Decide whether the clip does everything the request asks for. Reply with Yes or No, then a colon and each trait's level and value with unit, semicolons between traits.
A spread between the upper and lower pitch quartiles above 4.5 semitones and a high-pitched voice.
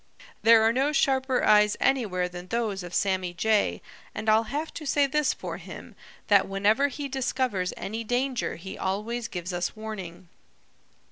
Yes: average, 5.3 semitones; high, 220 Hz